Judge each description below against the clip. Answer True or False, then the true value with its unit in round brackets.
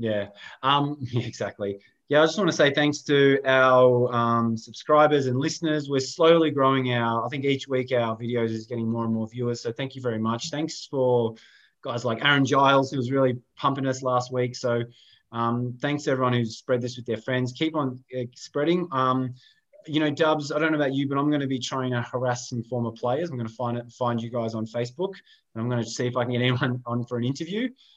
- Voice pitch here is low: True (125 Hz)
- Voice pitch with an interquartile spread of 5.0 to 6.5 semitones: False (3.2 semitones)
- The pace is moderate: False (235 wpm)